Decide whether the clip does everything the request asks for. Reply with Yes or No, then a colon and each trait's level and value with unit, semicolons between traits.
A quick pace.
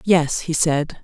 No: average, 175 wpm